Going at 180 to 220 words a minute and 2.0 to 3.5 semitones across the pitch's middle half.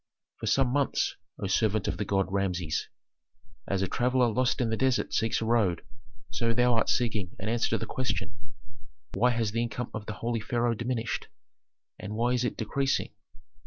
Yes: average, 185 wpm; average, 2.8 semitones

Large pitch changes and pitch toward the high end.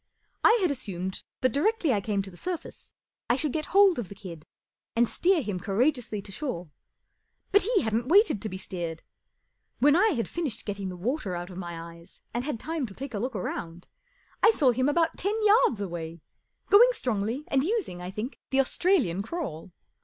Yes: wide, 8.8 semitones; high, 235 Hz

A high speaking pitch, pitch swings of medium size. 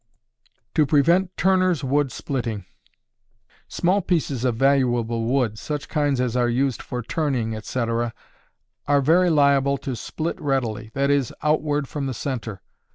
No: low, 135 Hz; average, 3.7 semitones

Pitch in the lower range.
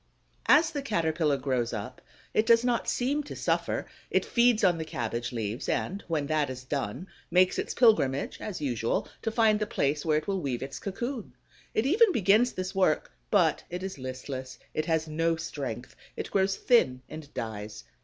No: medium, 160 Hz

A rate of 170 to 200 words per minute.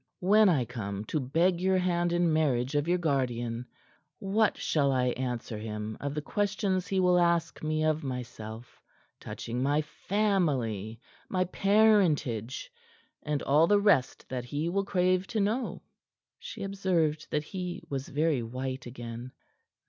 No: average, 150 wpm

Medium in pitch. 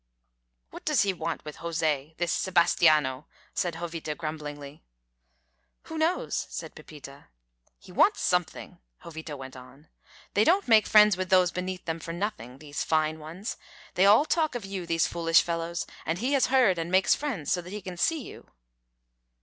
Yes: medium, 170 Hz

